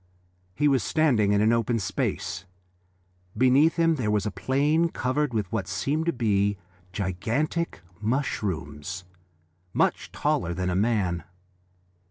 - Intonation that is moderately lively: No, wide, 6.3 semitones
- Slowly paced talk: Yes, slow, 130 wpm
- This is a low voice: Yes, low, 110 Hz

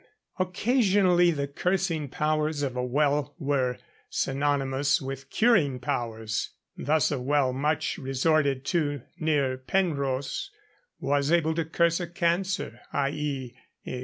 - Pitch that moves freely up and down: No, average, 3.8 semitones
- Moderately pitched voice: Yes, medium, 145 Hz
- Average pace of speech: No, slow, 115 wpm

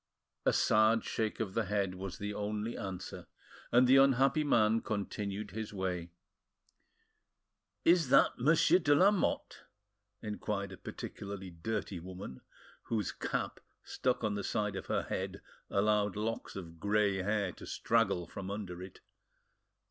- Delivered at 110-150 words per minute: Yes, average, 140 wpm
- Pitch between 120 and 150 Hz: No, low, 105 Hz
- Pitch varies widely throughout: No, average, 2.8 semitones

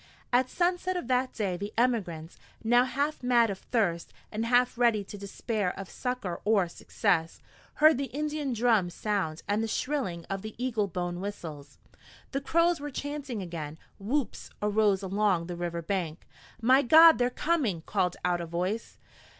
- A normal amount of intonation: No, wide, 6.0 semitones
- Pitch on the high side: Yes, high, 215 Hz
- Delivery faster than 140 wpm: Yes, average, 165 wpm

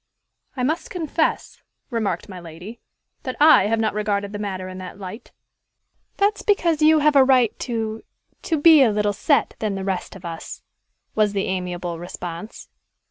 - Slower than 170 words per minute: No, average, 180 wpm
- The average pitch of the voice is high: Yes, high, 210 Hz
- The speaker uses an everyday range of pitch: No, wide, 6.5 semitones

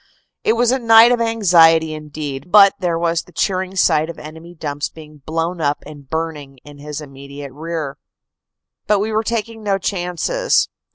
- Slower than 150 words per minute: No, average, 170 wpm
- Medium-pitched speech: Yes, medium, 165 Hz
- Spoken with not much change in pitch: No, average, 5.2 semitones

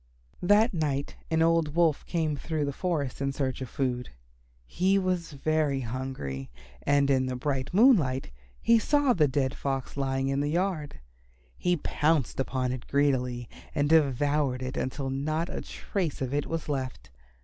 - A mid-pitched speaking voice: Yes, medium, 145 Hz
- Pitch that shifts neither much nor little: Yes, average, 3.7 semitones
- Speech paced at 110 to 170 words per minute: Yes, average, 160 wpm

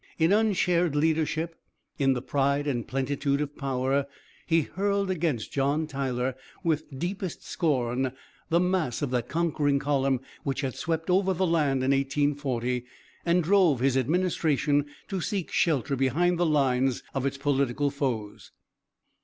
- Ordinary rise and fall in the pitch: Yes, average, 3.9 semitones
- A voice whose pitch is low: No, medium, 145 Hz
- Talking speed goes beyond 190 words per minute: No, average, 145 wpm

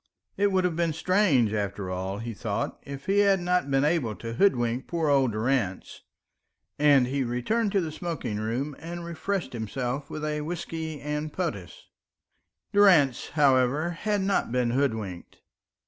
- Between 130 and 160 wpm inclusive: Yes, average, 155 wpm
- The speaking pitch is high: No, medium, 145 Hz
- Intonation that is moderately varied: No, wide, 6.2 semitones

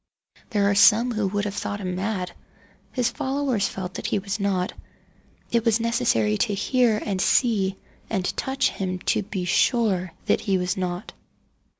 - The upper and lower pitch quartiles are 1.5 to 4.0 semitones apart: Yes, average, 3.4 semitones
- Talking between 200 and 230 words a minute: No, average, 170 wpm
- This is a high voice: Yes, high, 200 Hz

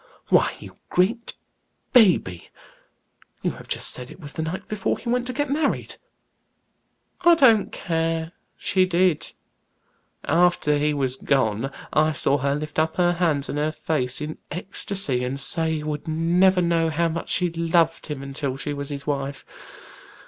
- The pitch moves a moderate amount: Yes, average, 4.0 semitones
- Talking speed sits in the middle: Yes, average, 165 wpm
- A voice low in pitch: No, medium, 160 Hz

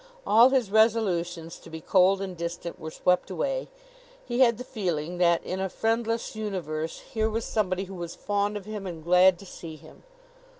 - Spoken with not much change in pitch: No, average, 4.1 semitones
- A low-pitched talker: No, high, 190 Hz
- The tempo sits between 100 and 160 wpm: No, average, 185 wpm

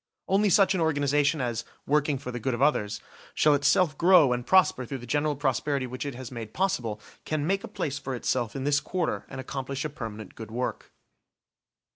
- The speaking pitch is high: No, medium, 140 Hz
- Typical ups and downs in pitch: Yes, average, 3.7 semitones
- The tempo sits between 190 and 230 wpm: Yes, average, 200 wpm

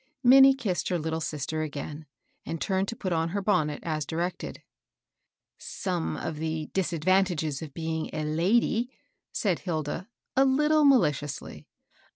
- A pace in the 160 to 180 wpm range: No, average, 145 wpm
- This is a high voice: No, medium, 165 Hz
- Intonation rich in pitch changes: No, average, 4.1 semitones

